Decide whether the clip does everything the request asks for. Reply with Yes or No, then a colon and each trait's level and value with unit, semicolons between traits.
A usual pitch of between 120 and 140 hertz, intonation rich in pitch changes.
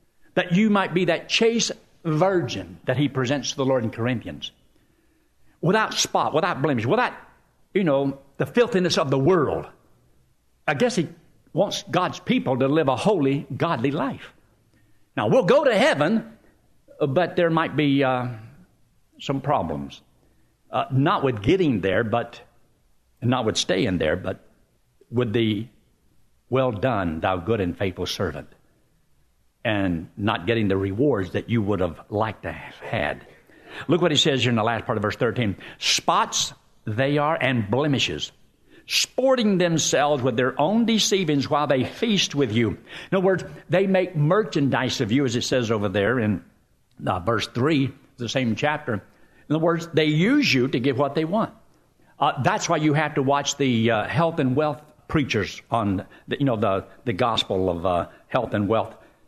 Yes: low, 135 Hz; wide, 6.0 semitones